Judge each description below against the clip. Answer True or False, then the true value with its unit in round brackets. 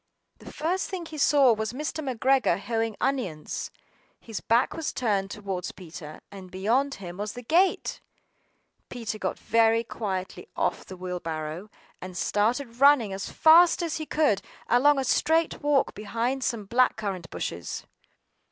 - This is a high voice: True (230 Hz)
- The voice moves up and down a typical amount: False (6.2 semitones)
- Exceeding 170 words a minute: False (155 wpm)